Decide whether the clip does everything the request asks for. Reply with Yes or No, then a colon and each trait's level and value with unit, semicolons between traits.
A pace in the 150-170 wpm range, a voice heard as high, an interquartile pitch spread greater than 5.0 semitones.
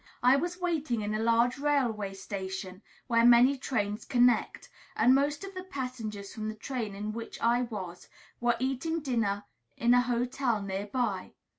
No: average, 165 wpm; high, 235 Hz; average, 3.9 semitones